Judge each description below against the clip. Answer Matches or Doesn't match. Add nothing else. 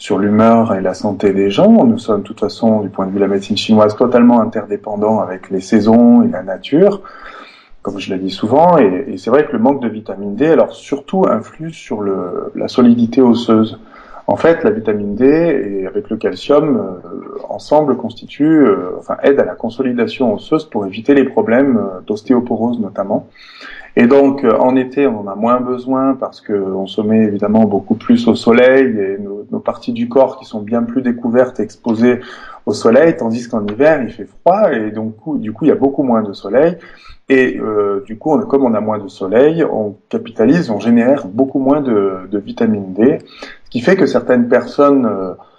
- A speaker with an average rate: Matches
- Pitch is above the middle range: Doesn't match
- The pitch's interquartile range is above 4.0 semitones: Matches